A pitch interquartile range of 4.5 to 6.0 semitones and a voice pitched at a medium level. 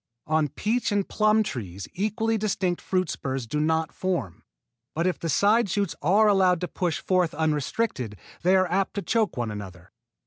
Yes: average, 5.3 semitones; medium, 180 Hz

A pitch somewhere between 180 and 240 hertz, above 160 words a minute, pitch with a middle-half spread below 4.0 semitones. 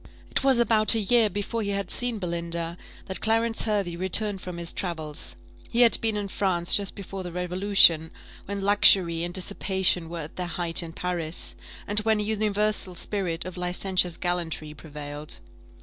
Yes: medium, 185 Hz; average, 170 wpm; average, 3.3 semitones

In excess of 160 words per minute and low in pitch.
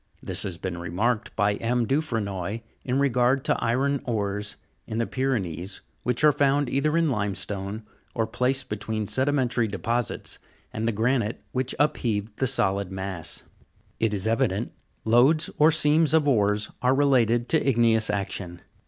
No: average, 155 wpm; low, 115 Hz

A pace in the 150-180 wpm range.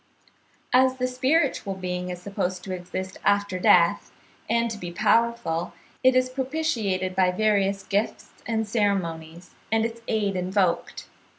No: slow, 135 wpm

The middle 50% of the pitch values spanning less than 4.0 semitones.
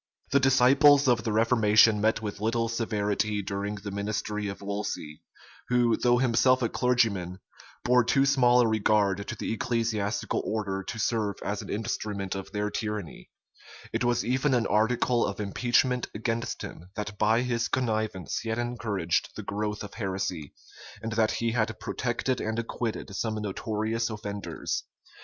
Yes: average, 2.7 semitones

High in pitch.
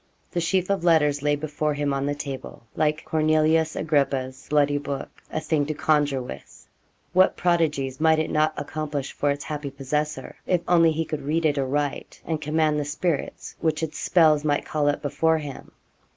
No: medium, 150 Hz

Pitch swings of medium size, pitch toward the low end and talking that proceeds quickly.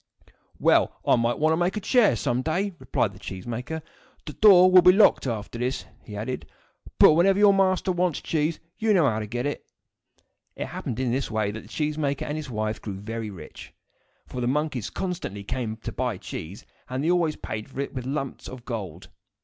No: wide, 7.1 semitones; low, 130 Hz; fast, 215 wpm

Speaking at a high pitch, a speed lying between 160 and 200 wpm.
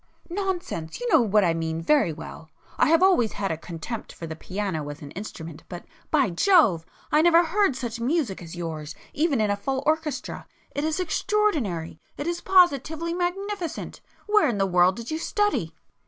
Yes: high, 245 Hz; average, 180 wpm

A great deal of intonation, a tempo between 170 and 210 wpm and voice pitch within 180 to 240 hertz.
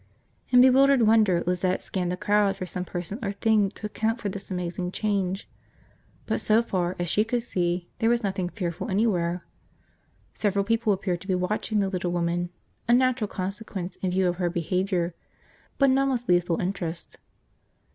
No: average, 3.6 semitones; average, 175 wpm; high, 190 Hz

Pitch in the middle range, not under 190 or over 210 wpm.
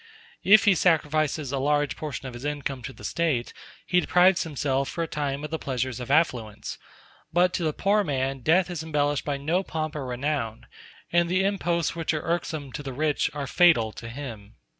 Yes: medium, 150 Hz; average, 200 wpm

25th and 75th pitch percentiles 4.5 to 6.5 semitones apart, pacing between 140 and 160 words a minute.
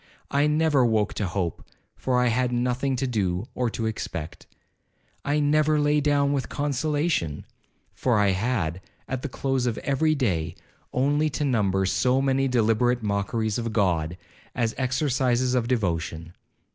Yes: average, 5.1 semitones; average, 150 wpm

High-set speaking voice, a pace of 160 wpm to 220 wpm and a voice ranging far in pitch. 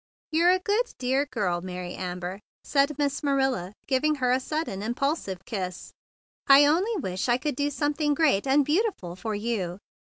Yes: very high, 265 Hz; average, 175 wpm; wide, 7.3 semitones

